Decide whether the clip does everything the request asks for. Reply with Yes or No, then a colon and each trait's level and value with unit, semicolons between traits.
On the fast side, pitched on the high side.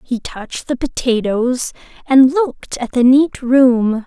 No: average, 150 wpm; very high, 255 Hz